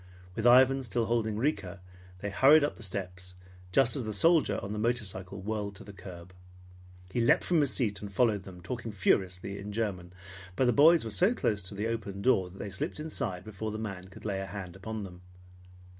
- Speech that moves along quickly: Yes, fast, 210 wpm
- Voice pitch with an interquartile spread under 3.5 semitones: No, average, 3.9 semitones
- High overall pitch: No, low, 105 Hz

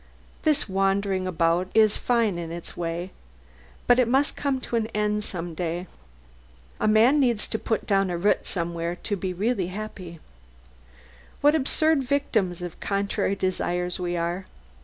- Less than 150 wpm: No, average, 155 wpm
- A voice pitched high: Yes, high, 195 Hz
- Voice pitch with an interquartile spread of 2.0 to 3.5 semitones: No, average, 4.2 semitones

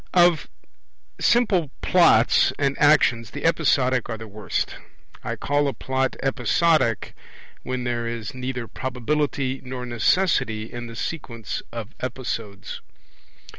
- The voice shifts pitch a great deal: No, average, 3.8 semitones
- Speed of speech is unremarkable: No, slow, 120 wpm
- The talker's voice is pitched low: Yes, low, 130 Hz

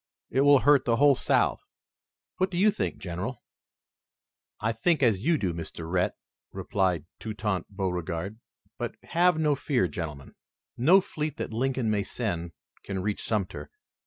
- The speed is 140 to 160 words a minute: Yes, average, 150 wpm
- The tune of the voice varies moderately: No, wide, 7.6 semitones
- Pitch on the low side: Yes, low, 110 Hz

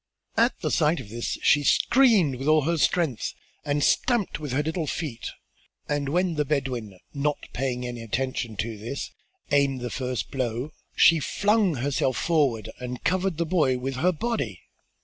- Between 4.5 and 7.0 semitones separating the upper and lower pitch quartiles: Yes, average, 4.9 semitones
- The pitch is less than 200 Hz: Yes, medium, 140 Hz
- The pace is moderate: Yes, average, 170 wpm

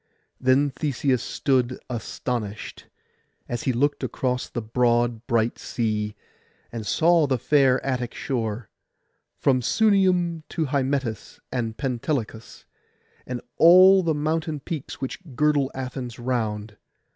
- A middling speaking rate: No, slow, 115 wpm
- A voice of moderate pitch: No, low, 130 Hz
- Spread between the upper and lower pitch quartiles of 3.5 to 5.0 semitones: Yes, average, 4.0 semitones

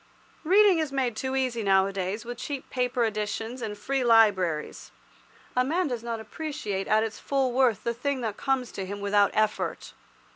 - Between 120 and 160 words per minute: No, average, 175 wpm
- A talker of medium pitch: No, high, 235 Hz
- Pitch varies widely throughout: No, average, 4.2 semitones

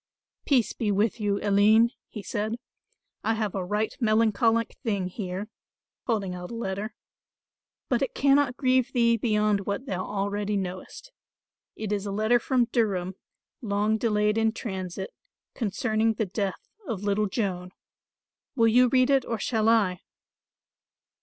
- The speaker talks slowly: No, average, 145 wpm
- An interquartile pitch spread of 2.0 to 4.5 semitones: Yes, narrow, 2.5 semitones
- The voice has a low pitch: No, high, 215 Hz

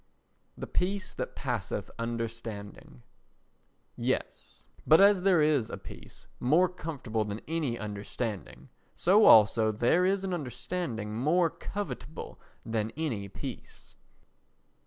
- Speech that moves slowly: Yes, slow, 115 wpm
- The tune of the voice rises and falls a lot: Yes, wide, 8.1 semitones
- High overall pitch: No, low, 125 Hz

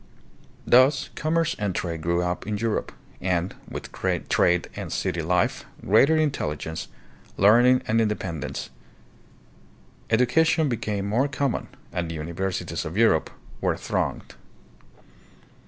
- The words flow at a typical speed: No, slow, 115 wpm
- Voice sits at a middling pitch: No, low, 105 Hz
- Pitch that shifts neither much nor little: No, wide, 6.5 semitones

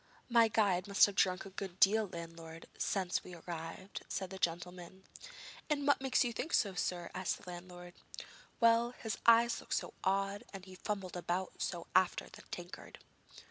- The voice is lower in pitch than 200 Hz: Yes, high, 190 Hz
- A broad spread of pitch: No, average, 3.0 semitones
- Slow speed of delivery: No, average, 180 wpm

